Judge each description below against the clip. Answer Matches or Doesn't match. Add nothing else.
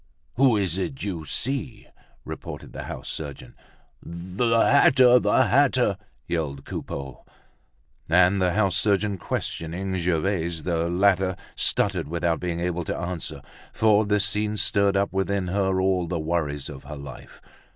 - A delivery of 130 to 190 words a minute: Matches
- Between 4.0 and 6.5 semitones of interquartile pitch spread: Doesn't match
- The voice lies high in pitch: Doesn't match